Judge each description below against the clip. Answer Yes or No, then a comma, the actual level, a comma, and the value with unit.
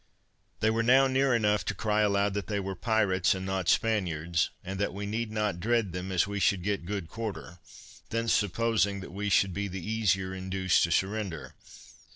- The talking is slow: No, average, 190 wpm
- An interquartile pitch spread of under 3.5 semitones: Yes, average, 2.7 semitones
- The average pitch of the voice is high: No, low, 100 Hz